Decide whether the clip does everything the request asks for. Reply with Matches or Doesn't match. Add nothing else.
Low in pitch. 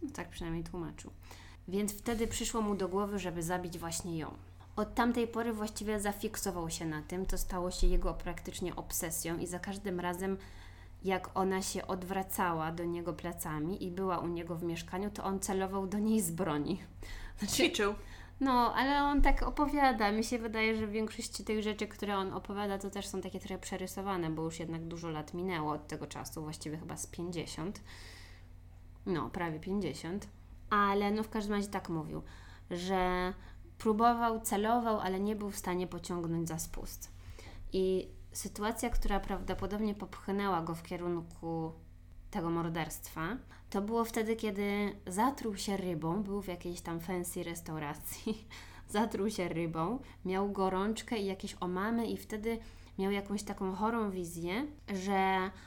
Doesn't match